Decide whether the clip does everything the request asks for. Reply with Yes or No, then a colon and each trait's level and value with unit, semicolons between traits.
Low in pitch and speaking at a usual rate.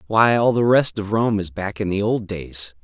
No: low, 105 Hz; fast, 255 wpm